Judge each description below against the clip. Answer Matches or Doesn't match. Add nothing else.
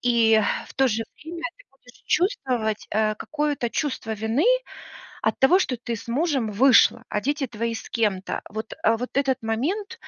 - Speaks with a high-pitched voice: Matches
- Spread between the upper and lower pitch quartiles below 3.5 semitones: Doesn't match